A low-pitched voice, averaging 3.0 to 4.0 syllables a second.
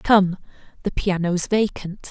No: high, 190 Hz; 3.7 syllables/s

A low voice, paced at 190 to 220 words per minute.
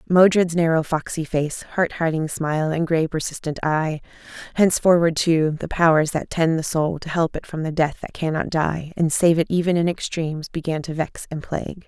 No: medium, 160 Hz; average, 195 wpm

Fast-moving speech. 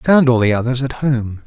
Yes: fast, 285 wpm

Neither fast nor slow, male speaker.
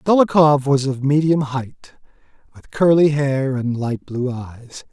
Yes: average, 145 wpm; male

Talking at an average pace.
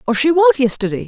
No: fast, 225 wpm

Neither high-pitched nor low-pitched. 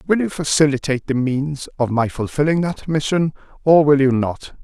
Yes: medium, 145 Hz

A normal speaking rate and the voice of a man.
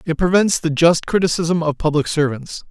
Yes: average, 175 wpm; male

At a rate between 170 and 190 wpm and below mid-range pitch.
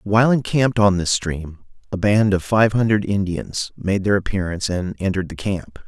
Yes: average, 185 wpm; low, 100 Hz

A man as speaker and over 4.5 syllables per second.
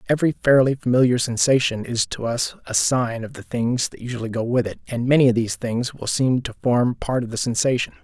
Yes: male; 5.7 syllables/s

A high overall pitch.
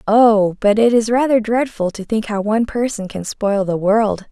Yes: high, 215 Hz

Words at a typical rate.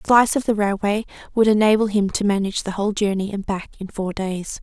No: fast, 235 wpm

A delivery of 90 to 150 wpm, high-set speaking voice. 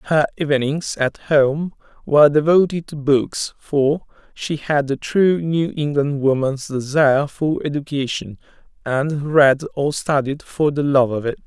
No: average, 145 wpm; medium, 145 Hz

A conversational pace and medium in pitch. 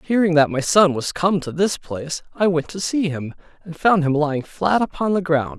No: fast, 235 wpm; medium, 165 Hz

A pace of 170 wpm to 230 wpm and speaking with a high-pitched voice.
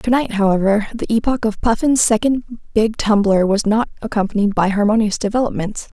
No: average, 160 wpm; high, 215 Hz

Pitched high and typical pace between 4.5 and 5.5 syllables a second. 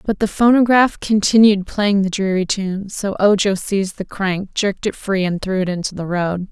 Yes: high, 195 Hz; 4.9 syllables/s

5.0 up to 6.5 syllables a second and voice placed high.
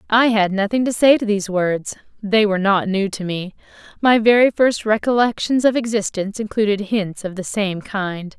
Yes: 5.1 syllables/s; high, 210 Hz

